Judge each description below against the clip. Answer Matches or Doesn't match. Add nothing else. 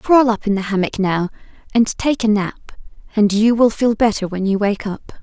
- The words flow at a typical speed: Doesn't match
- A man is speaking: Doesn't match